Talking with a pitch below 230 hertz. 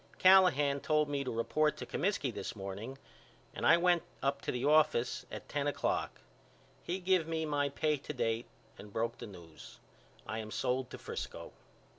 Yes: medium, 140 Hz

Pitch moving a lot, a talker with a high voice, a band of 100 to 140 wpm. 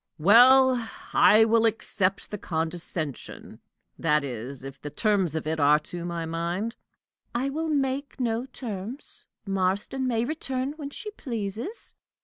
Yes: wide, 7.7 semitones; high, 215 Hz; slow, 135 wpm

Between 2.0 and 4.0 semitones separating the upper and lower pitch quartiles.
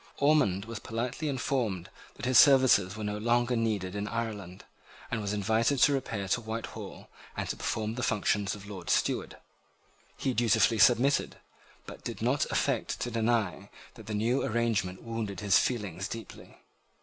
Yes: average, 2.9 semitones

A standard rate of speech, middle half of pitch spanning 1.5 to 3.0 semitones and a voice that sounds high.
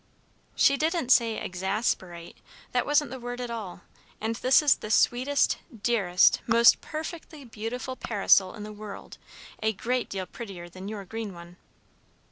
No: average, 150 wpm; average, 4.4 semitones; high, 225 Hz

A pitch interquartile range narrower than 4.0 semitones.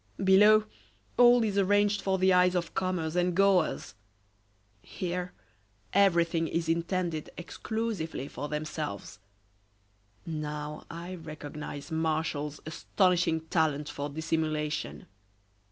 Yes: average, 3.4 semitones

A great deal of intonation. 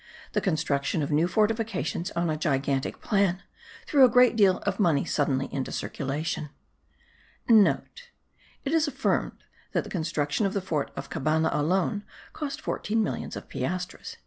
Yes: wide, 5.9 semitones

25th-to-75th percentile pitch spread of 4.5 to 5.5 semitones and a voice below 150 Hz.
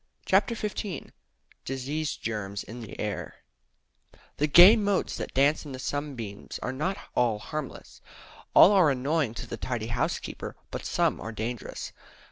Yes: average, 5.2 semitones; low, 135 Hz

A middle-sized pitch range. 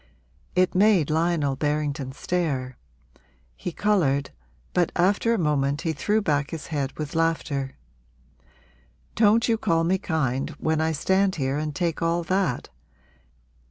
Yes: average, 4.1 semitones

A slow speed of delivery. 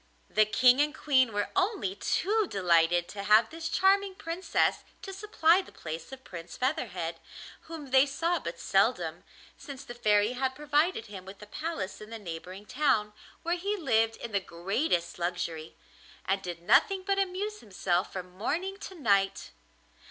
No: average, 165 wpm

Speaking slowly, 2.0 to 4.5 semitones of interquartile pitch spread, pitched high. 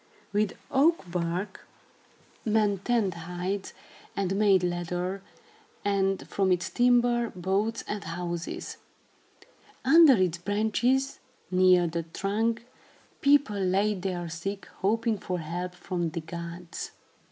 Yes: slow, 110 wpm; average, 3.5 semitones; high, 195 Hz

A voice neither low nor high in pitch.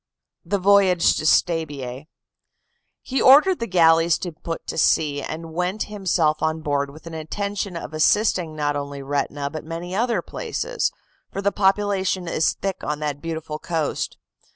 Yes: medium, 165 Hz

